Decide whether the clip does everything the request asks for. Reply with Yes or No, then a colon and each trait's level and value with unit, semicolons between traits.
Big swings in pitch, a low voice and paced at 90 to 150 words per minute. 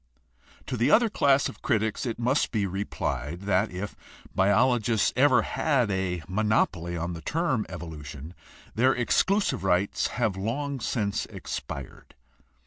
Yes: wide, 5.7 semitones; low, 105 Hz; slow, 135 wpm